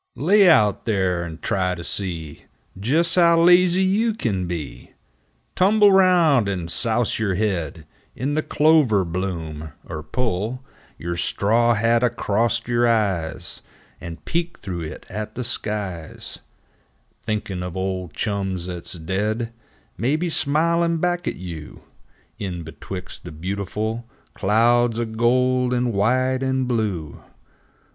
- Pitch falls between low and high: No, low, 110 Hz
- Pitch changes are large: Yes, wide, 5.9 semitones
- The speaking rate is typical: No, slow, 130 wpm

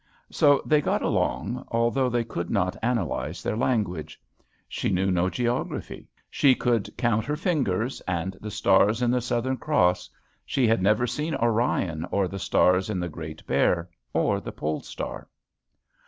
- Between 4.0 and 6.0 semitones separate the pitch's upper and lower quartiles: Yes, average, 5.3 semitones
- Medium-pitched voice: No, low, 110 Hz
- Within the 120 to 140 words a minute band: No, average, 160 wpm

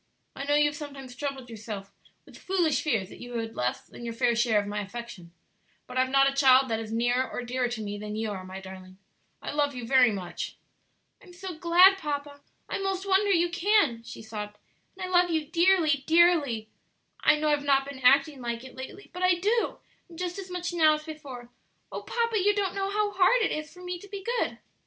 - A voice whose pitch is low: No, very high, 285 Hz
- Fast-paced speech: Yes, fast, 225 wpm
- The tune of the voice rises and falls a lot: Yes, wide, 7.1 semitones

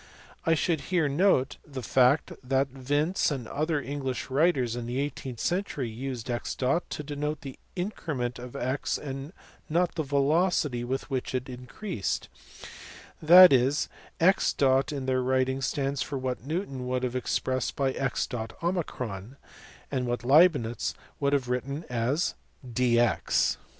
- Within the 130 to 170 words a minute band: Yes, average, 140 wpm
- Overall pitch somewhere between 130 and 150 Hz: Yes, low, 135 Hz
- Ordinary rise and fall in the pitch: Yes, average, 3.1 semitones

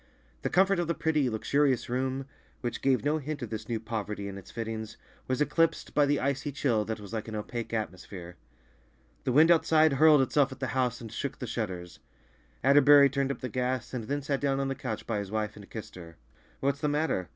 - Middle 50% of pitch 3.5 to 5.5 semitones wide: Yes, average, 4.5 semitones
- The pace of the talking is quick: Yes, fast, 220 wpm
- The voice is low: Yes, low, 130 Hz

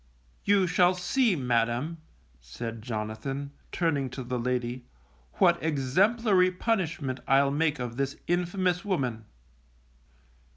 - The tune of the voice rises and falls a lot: Yes, wide, 6.4 semitones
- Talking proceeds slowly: Yes, slow, 110 wpm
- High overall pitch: No, medium, 140 Hz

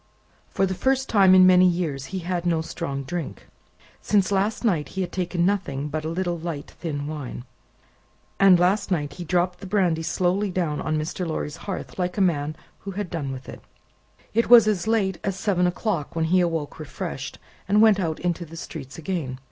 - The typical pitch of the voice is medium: Yes, medium, 175 Hz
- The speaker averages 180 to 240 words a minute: Yes, average, 200 wpm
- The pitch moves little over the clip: No, average, 3.4 semitones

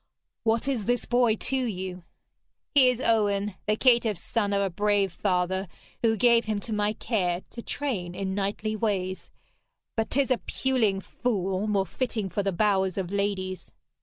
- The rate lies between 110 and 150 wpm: No, average, 165 wpm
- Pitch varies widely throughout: No, average, 3.3 semitones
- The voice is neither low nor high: No, high, 205 Hz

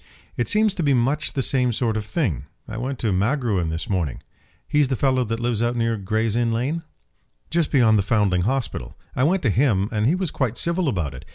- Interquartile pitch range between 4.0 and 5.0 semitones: Yes, average, 4.6 semitones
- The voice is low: Yes, low, 120 Hz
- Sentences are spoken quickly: Yes, fast, 220 wpm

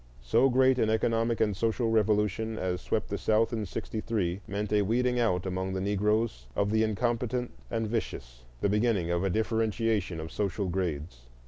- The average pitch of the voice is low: Yes, low, 105 Hz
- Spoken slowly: No, average, 175 wpm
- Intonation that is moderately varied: Yes, average, 3.3 semitones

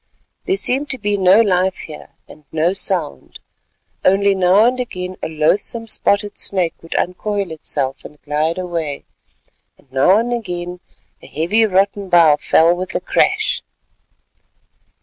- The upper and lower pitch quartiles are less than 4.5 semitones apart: Yes, average, 4.1 semitones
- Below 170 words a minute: Yes, average, 140 wpm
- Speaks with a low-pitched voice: No, medium, 185 Hz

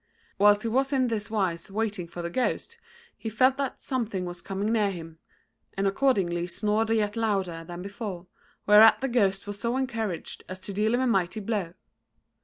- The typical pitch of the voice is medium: No, high, 210 Hz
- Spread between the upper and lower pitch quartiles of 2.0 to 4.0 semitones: Yes, average, 3.7 semitones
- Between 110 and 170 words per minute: No, average, 185 wpm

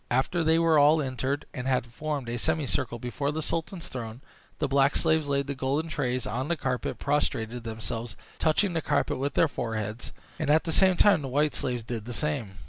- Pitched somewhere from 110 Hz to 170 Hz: Yes, medium, 140 Hz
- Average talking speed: No, fast, 210 wpm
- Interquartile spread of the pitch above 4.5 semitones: No, average, 4.2 semitones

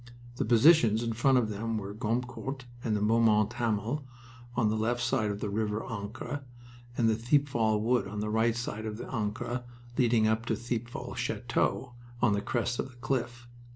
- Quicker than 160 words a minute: Yes, average, 175 wpm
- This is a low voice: Yes, low, 115 Hz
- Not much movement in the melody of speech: Yes, narrow, 2.1 semitones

